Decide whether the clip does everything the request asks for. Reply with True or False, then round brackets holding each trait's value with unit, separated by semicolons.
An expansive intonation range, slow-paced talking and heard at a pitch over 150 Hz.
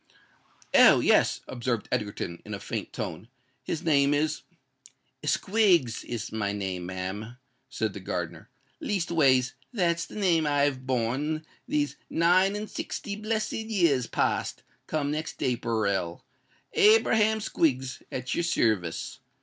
False (7.5 semitones; 120 wpm; 140 Hz)